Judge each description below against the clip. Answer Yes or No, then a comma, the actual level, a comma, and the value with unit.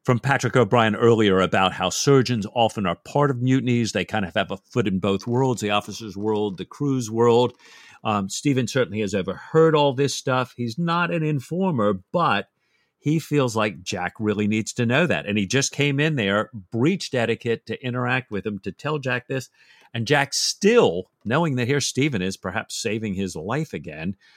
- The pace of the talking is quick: No, average, 190 wpm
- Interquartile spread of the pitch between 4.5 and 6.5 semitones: Yes, average, 5.0 semitones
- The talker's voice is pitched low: Yes, low, 120 Hz